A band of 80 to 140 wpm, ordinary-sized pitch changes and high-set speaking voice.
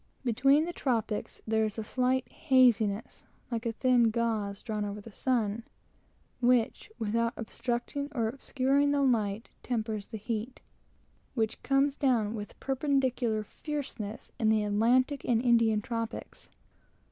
Yes: slow, 135 wpm; average, 3.0 semitones; high, 230 Hz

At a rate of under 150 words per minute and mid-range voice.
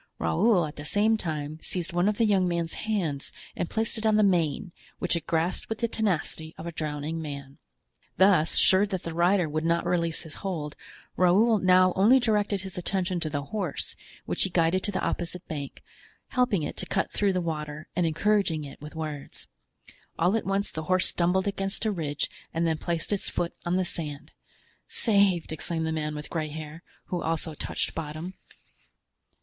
No: average, 190 wpm; medium, 175 Hz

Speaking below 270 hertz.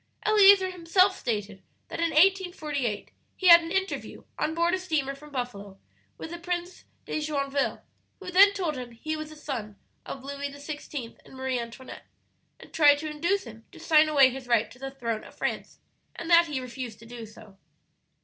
No: very high, 290 Hz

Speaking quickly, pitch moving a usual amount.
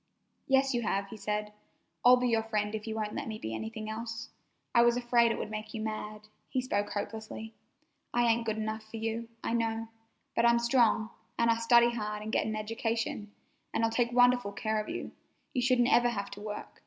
No: fast, 215 wpm; narrow, 1.8 semitones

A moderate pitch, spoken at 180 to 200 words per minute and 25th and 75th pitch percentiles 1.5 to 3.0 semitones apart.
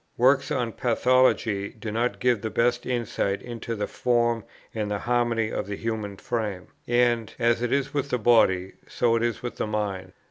No: low, 115 Hz; average, 185 wpm; narrow, 2.5 semitones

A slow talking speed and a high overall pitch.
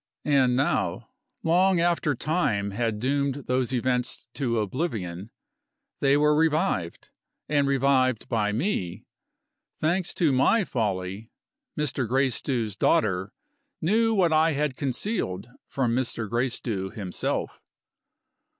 No: slow, 110 wpm; low, 130 Hz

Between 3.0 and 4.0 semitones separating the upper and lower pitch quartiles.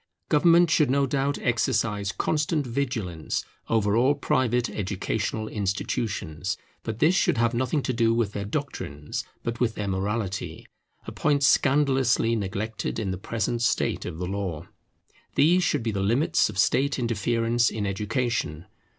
No: average, 4.9 semitones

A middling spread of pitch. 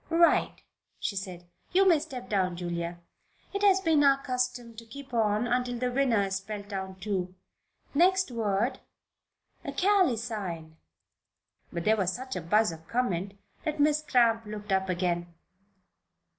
No: wide, 6.0 semitones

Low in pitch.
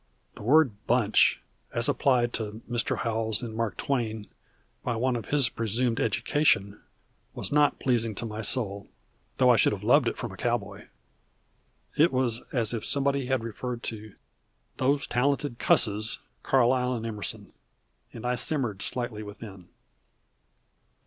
Yes: low, 120 Hz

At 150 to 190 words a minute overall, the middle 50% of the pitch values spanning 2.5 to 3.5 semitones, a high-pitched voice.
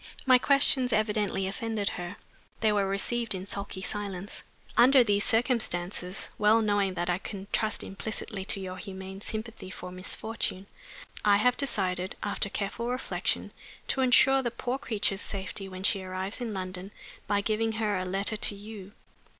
Yes: average, 160 wpm; average, 2.8 semitones; high, 205 Hz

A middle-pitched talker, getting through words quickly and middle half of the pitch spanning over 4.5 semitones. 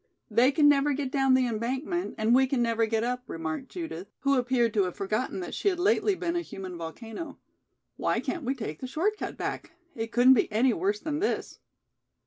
No: very high, 255 Hz; fast, 210 wpm; average, 4.9 semitones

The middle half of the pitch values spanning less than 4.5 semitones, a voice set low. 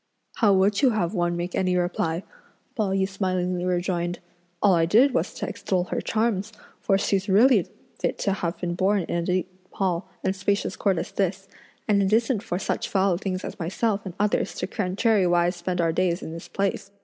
No: narrow, 2.4 semitones; high, 190 Hz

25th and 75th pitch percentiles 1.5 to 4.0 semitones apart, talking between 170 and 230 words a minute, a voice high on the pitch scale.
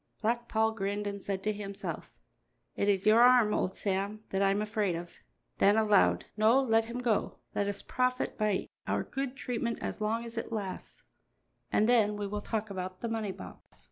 Yes: narrow, 2.4 semitones; average, 195 wpm; high, 215 Hz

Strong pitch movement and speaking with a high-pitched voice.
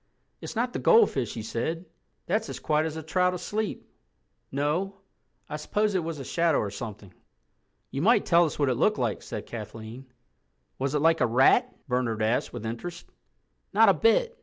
No: wide, 7.4 semitones; medium, 150 Hz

